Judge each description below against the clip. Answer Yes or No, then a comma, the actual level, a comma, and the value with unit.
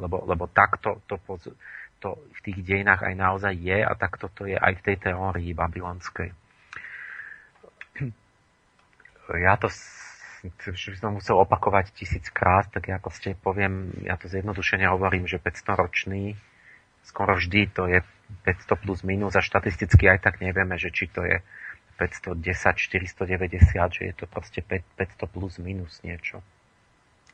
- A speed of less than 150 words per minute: Yes, average, 140 wpm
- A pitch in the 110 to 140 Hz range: No, very low, 95 Hz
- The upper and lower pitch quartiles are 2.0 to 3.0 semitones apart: No, narrow, 1.4 semitones